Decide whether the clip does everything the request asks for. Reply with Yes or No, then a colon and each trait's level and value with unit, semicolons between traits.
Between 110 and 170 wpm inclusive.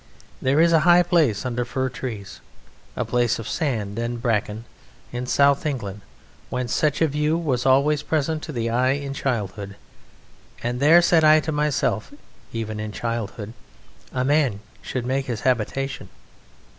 Yes: average, 155 wpm